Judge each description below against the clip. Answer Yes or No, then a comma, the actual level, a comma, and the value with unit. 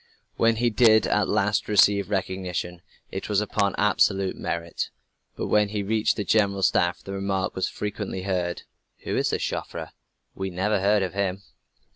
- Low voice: Yes, low, 100 Hz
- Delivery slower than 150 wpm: No, average, 165 wpm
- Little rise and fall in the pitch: Yes, narrow, 1.8 semitones